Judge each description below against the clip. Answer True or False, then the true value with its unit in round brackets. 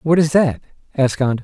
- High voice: False (145 Hz)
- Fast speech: True (210 wpm)